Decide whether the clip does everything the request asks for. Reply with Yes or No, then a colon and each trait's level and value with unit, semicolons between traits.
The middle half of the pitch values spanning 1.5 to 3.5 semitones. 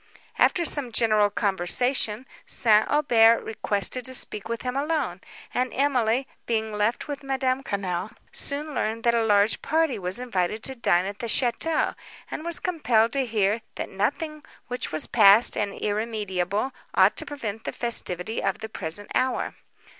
No: average, 4.2 semitones